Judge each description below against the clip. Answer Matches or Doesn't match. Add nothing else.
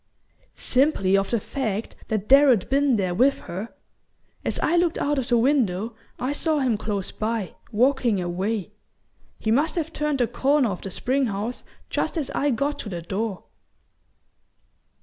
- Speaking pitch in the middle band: Doesn't match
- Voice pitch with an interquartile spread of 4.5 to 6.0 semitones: Matches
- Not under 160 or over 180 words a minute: Matches